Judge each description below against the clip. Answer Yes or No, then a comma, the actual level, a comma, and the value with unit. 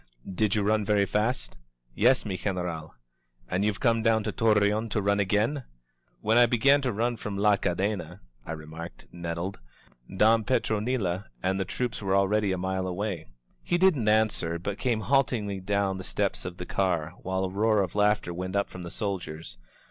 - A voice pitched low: Yes, low, 100 Hz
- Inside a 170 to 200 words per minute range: Yes, average, 180 wpm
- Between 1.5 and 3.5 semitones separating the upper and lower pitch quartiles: Yes, average, 3.0 semitones